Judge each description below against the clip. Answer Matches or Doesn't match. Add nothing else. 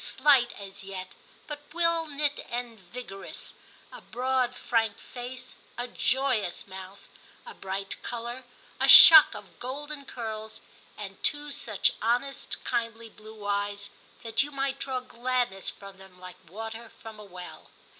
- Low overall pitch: Doesn't match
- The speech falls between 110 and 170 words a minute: Matches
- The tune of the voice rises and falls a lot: Doesn't match